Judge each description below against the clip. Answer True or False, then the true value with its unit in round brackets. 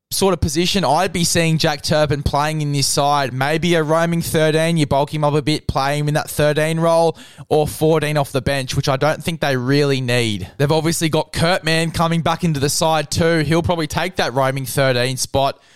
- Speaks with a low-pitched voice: False (150 Hz)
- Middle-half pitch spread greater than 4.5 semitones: False (3.0 semitones)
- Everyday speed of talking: False (220 wpm)